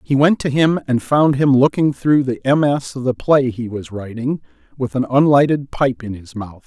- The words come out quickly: Yes, fast, 215 wpm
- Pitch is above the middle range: No, low, 130 Hz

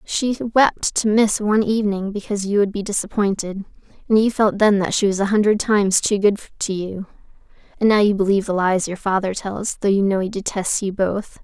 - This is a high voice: Yes, high, 200 Hz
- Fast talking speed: Yes, fast, 215 wpm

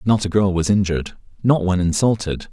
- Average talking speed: Yes, average, 190 wpm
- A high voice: No, very low, 95 Hz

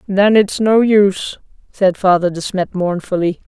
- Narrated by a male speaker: No, female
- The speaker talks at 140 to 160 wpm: Yes, average, 150 wpm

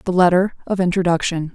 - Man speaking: No, female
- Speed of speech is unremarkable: Yes, average, 155 wpm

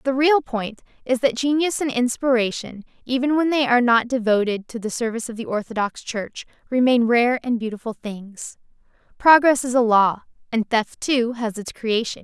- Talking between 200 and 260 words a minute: No, average, 170 wpm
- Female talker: Yes, female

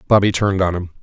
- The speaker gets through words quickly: Yes, fast, 235 wpm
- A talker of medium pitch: No, very low, 95 Hz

